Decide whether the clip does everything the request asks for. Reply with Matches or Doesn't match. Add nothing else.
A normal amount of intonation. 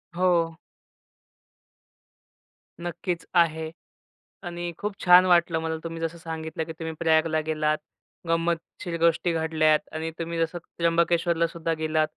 Doesn't match